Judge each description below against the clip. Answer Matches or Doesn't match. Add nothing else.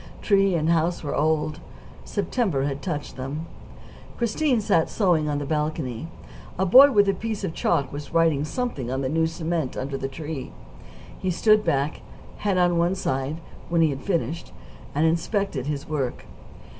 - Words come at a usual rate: Matches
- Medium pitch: Matches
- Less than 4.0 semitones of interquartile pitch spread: Doesn't match